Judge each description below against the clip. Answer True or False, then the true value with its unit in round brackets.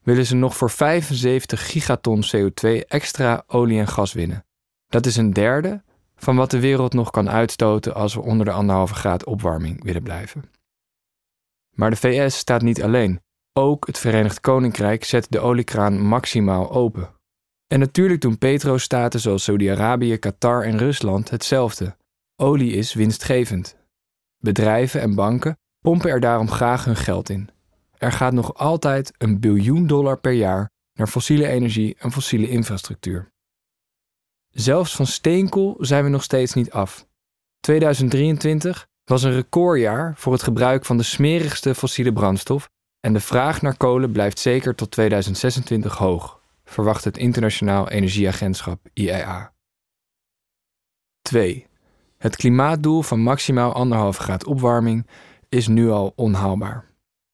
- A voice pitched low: True (120 Hz)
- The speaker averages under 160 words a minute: True (140 wpm)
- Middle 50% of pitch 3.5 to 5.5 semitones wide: True (4.2 semitones)